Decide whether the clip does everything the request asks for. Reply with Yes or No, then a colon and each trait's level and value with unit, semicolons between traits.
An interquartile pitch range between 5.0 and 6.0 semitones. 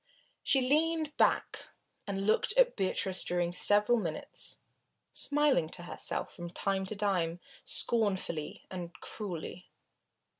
Yes: wide, 5.5 semitones